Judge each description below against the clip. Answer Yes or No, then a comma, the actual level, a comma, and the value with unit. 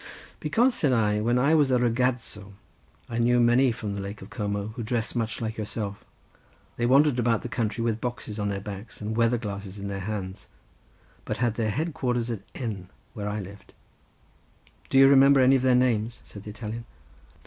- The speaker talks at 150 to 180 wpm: No, average, 195 wpm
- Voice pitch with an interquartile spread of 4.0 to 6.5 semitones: No, average, 3.1 semitones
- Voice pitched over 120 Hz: No, low, 115 Hz